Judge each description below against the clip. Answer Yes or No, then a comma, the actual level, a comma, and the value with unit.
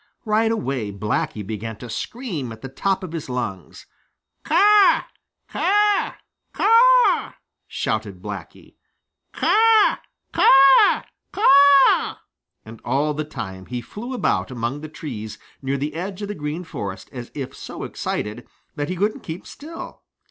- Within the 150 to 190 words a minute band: No, slow, 135 wpm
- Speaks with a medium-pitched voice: Yes, medium, 155 Hz